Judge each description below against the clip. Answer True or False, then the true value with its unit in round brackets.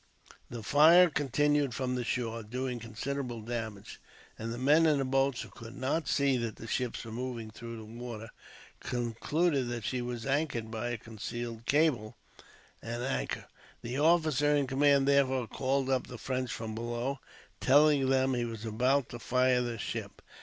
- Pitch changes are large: False (3.1 semitones)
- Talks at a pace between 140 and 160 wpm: False (170 wpm)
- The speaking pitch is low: True (125 Hz)